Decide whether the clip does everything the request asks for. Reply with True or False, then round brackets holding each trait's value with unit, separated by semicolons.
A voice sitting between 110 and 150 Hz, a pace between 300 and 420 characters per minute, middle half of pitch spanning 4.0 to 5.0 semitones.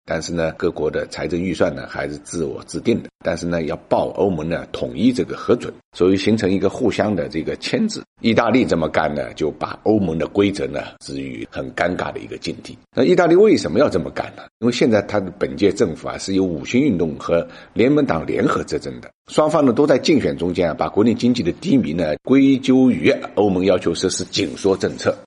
False (90 Hz; 330 characters per minute; 4.4 semitones)